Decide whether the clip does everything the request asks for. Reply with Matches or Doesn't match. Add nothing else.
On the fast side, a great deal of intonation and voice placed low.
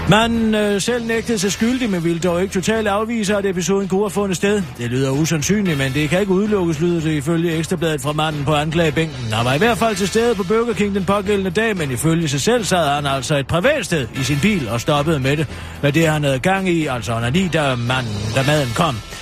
Doesn't match